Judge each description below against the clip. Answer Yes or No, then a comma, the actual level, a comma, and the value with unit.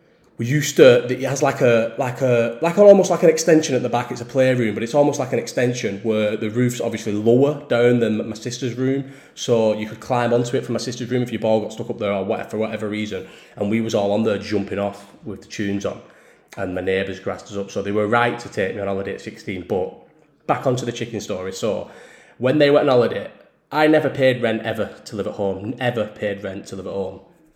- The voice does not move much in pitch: No, average, 3.5 semitones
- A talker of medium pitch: No, low, 115 Hz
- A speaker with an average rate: No, fast, 255 wpm